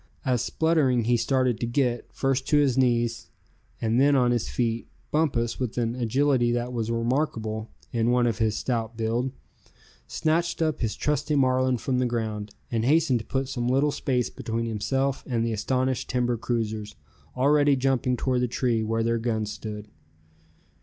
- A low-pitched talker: Yes, low, 120 Hz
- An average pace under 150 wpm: No, average, 170 wpm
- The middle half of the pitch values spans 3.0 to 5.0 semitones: No, narrow, 2.6 semitones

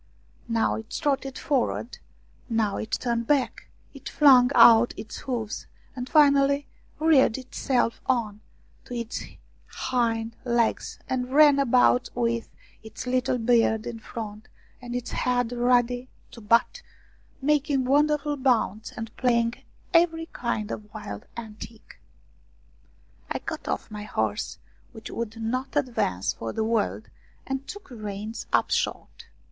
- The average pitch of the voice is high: Yes, high, 240 Hz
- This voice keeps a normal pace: No, slow, 130 wpm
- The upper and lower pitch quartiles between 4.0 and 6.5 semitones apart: No, average, 3.0 semitones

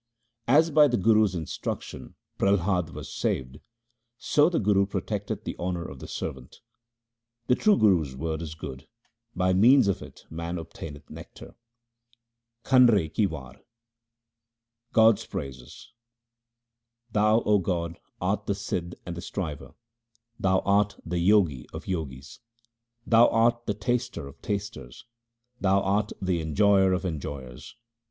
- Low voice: Yes, very low, 95 Hz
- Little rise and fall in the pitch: No, average, 5.2 semitones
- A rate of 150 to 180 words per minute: No, average, 140 wpm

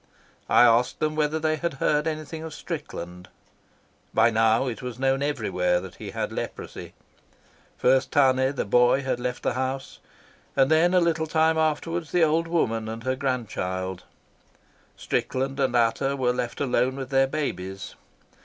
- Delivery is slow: No, average, 160 wpm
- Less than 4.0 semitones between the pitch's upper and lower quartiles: No, average, 4.4 semitones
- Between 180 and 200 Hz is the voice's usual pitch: No, low, 135 Hz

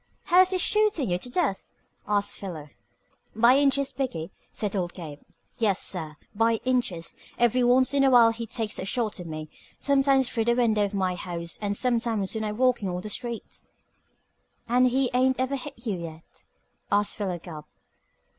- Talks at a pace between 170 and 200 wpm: Yes, average, 180 wpm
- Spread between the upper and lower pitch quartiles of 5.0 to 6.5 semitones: Yes, wide, 5.4 semitones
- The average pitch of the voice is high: Yes, high, 225 Hz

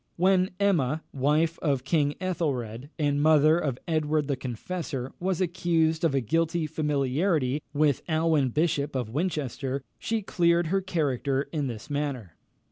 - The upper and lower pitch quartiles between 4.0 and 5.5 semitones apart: No, average, 3.5 semitones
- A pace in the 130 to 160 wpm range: Yes, average, 145 wpm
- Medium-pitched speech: Yes, medium, 150 Hz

